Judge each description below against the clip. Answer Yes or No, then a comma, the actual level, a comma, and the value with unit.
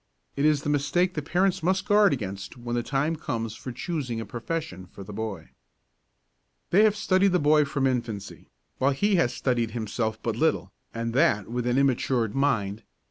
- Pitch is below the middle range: Yes, low, 130 Hz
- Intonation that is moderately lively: No, wide, 6.0 semitones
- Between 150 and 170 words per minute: No, average, 185 wpm